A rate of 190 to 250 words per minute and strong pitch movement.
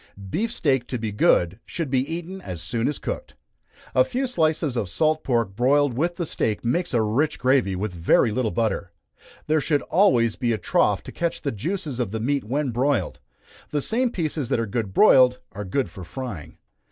Yes: average, 200 wpm; wide, 5.8 semitones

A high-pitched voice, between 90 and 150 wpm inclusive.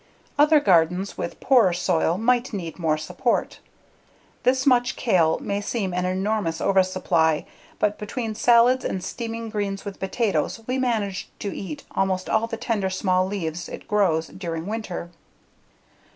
Yes: high, 195 Hz; average, 145 wpm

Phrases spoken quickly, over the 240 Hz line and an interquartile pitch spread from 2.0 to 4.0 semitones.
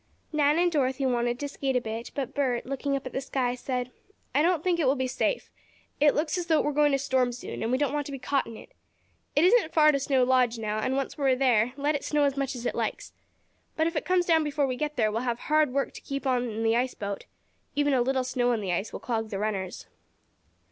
Yes: fast, 270 wpm; very high, 265 Hz; average, 3.1 semitones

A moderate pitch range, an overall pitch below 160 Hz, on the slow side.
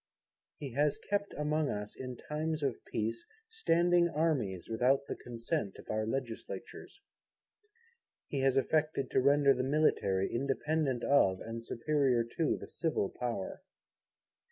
Yes: average, 4.8 semitones; low, 135 Hz; slow, 130 wpm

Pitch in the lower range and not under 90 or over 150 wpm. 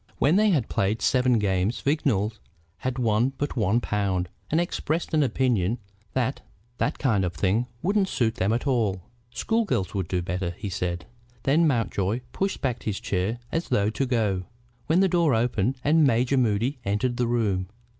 No: low, 115 Hz; average, 175 wpm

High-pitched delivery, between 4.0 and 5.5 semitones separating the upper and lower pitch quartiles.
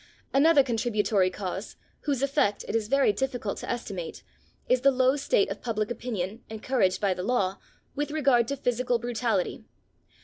Yes: high, 235 Hz; average, 4.5 semitones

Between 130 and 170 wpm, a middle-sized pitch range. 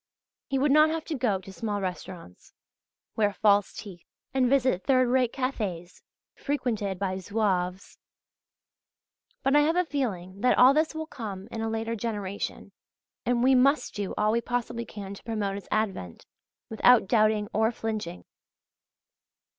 Yes: average, 155 wpm; average, 4.4 semitones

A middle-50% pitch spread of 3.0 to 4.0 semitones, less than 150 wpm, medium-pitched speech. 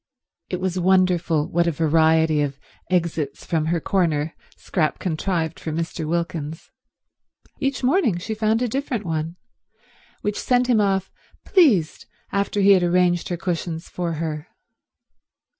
Yes: average, 3.6 semitones; average, 140 wpm; medium, 175 Hz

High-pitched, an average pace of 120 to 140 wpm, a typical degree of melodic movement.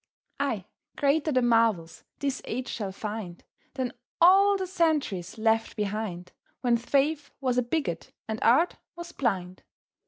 No: high, 240 Hz; slow, 135 wpm; wide, 5.7 semitones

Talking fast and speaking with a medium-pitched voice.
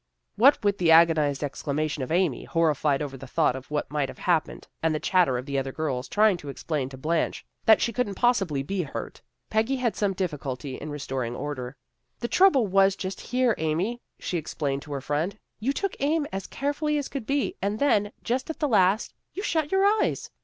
Yes: fast, 220 wpm; medium, 175 Hz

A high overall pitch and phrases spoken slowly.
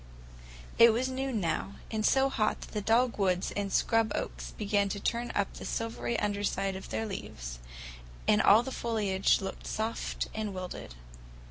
No: high, 210 Hz; average, 165 wpm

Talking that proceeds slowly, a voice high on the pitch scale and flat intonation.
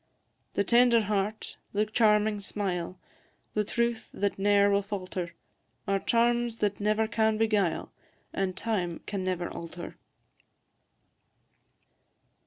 Yes: slow, 110 wpm; high, 205 Hz; narrow, 2.2 semitones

